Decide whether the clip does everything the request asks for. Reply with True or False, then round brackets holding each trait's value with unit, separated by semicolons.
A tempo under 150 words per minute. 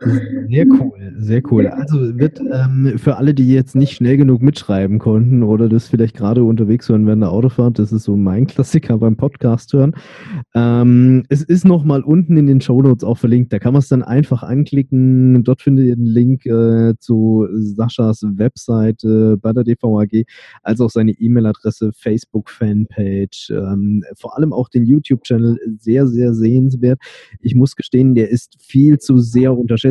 False (175 wpm)